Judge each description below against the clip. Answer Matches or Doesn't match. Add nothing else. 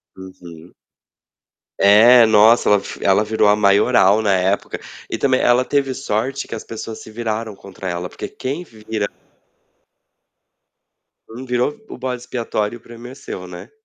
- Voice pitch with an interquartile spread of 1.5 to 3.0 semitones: Doesn't match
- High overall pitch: Doesn't match